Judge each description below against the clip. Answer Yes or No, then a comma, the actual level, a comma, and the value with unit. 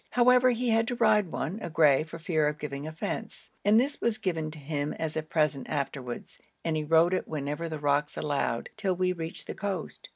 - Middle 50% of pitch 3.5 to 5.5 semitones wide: Yes, average, 5.2 semitones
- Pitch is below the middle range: No, medium, 160 Hz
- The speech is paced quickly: Yes, fast, 215 wpm